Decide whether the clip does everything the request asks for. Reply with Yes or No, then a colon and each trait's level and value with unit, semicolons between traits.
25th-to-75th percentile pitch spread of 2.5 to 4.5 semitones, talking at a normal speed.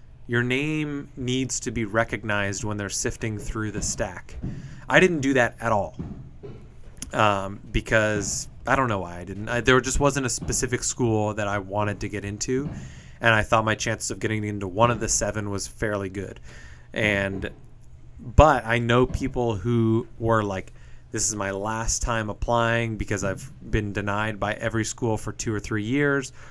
Yes: average, 3.1 semitones; average, 180 wpm